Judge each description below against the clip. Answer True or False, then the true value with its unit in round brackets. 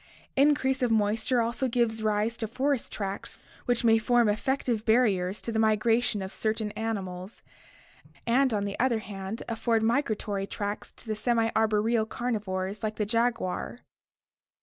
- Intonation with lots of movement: False (2.4 semitones)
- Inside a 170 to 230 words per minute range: False (150 wpm)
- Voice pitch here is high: True (225 Hz)